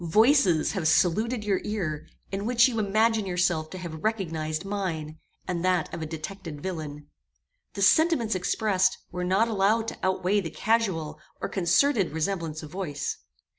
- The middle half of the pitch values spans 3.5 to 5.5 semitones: Yes, average, 5.0 semitones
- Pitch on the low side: No, medium, 185 Hz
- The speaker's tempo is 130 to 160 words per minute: Yes, average, 155 wpm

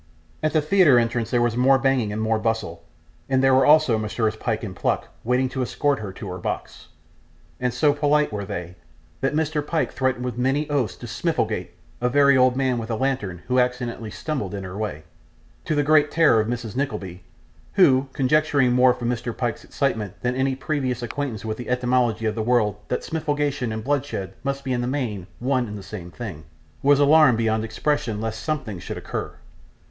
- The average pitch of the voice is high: No, low, 125 Hz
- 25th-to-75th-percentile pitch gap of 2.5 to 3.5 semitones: No, average, 4.0 semitones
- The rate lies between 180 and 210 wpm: Yes, average, 200 wpm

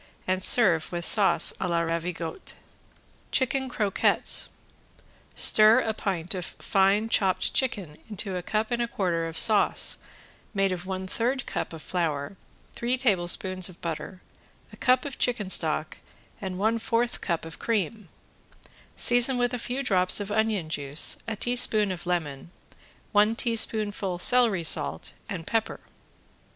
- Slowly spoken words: No, average, 145 wpm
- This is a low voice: No, high, 195 Hz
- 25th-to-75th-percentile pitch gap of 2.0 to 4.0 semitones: No, average, 4.8 semitones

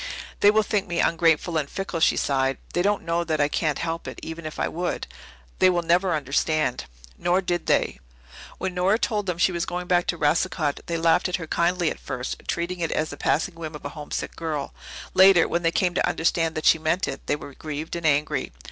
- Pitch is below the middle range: No, medium, 165 Hz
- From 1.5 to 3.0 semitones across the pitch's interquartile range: Yes, narrow, 2.5 semitones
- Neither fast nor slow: No, fast, 230 wpm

